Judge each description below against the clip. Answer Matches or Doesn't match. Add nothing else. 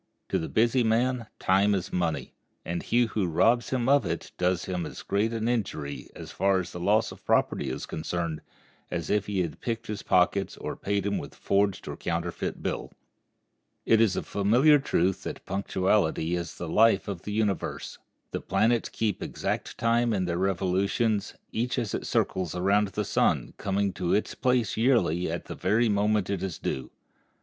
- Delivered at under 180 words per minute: Doesn't match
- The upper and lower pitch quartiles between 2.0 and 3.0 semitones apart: Doesn't match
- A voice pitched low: Matches